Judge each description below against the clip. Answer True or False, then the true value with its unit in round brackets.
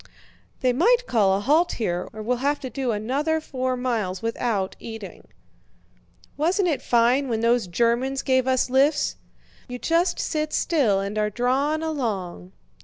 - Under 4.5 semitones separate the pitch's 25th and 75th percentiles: False (4.8 semitones)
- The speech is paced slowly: False (155 wpm)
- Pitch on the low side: False (250 Hz)